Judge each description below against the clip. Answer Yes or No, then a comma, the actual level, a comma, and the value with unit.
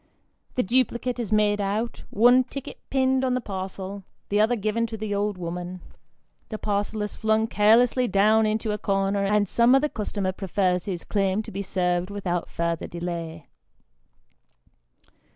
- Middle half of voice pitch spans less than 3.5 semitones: Yes, average, 2.9 semitones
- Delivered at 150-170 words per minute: Yes, average, 155 wpm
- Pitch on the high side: Yes, high, 205 Hz